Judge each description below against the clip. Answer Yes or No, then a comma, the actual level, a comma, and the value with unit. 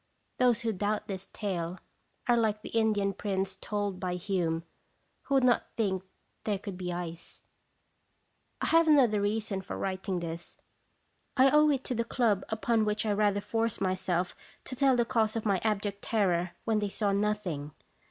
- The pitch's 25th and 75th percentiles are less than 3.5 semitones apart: Yes, average, 3.1 semitones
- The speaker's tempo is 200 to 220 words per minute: No, average, 175 wpm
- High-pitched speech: Yes, high, 205 Hz